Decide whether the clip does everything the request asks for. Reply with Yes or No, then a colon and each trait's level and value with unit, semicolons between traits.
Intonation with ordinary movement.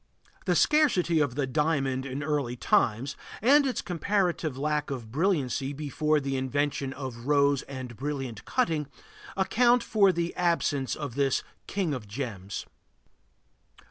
Yes: average, 4.4 semitones